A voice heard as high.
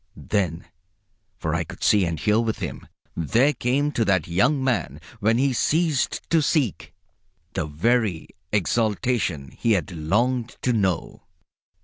No: low, 110 Hz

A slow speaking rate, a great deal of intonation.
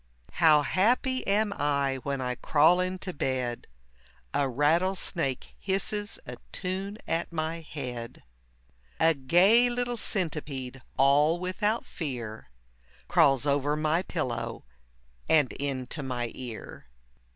Yes: slow, 110 wpm; wide, 5.7 semitones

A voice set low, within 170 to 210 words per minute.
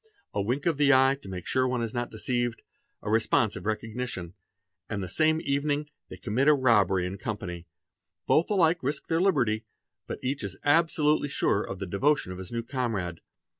Yes: low, 120 Hz; average, 185 wpm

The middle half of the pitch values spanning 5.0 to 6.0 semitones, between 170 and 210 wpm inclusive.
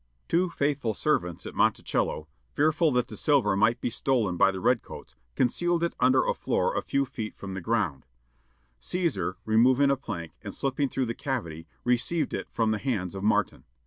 Yes: wide, 5.6 semitones; average, 185 wpm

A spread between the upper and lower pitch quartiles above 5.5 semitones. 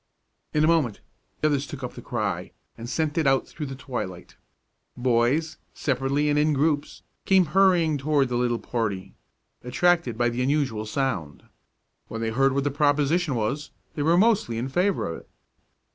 No: average, 4.2 semitones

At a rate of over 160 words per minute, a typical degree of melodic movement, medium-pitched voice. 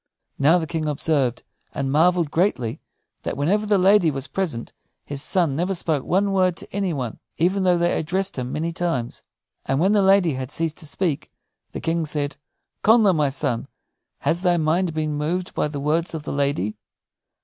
Yes: average, 185 wpm; average, 4.2 semitones; medium, 160 Hz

